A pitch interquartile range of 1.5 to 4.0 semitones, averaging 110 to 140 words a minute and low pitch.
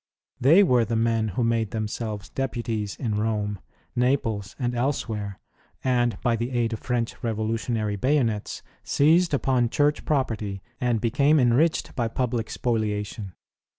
Yes: average, 2.8 semitones; slow, 135 wpm; low, 115 Hz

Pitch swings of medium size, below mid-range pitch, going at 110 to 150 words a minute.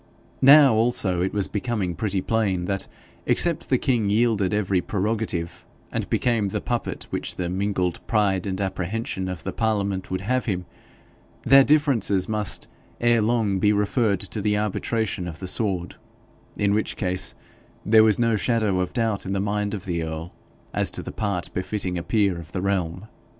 No: average, 3.2 semitones; low, 100 Hz; average, 175 wpm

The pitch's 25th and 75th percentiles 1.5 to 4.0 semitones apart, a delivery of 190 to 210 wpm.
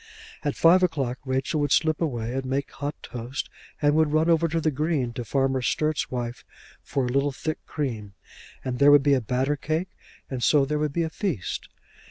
Yes: average, 3.3 semitones; average, 200 wpm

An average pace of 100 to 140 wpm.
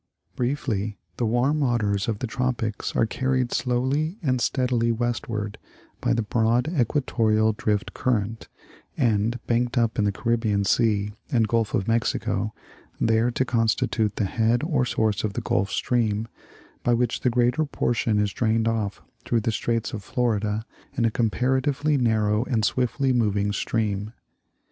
No: average, 150 wpm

